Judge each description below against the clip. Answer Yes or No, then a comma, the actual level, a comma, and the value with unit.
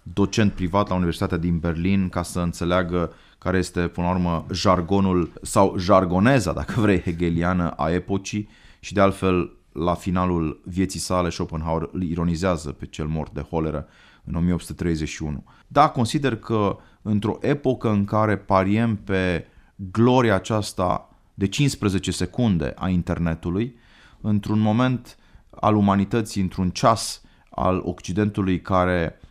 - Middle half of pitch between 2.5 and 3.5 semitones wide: Yes, average, 3.2 semitones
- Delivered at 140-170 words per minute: No, average, 130 wpm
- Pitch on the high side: No, very low, 95 Hz